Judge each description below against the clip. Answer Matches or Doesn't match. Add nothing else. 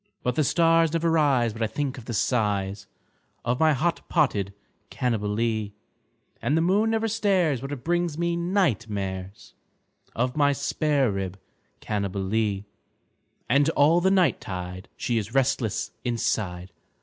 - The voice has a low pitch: Matches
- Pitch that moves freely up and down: Matches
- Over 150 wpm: Doesn't match